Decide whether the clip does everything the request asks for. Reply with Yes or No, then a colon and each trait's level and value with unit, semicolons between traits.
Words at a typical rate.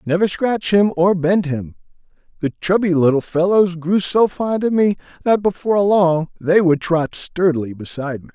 Yes: average, 175 wpm